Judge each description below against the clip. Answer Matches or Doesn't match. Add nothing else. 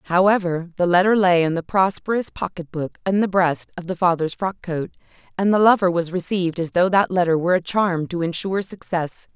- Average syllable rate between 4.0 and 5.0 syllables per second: Doesn't match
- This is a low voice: Doesn't match